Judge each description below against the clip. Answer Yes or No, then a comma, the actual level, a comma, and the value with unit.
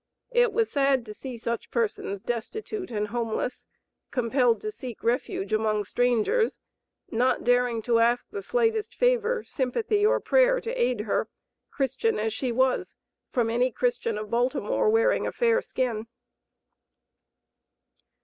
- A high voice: Yes, very high, 250 Hz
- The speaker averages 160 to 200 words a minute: No, average, 140 wpm